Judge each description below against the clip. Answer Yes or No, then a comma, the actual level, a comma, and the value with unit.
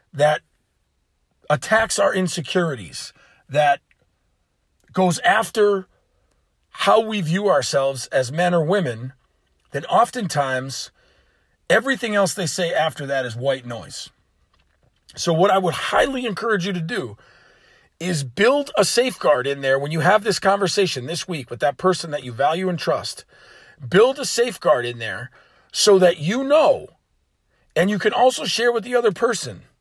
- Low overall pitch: No, medium, 175 Hz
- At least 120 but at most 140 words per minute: No, average, 150 wpm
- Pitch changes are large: Yes, wide, 7.4 semitones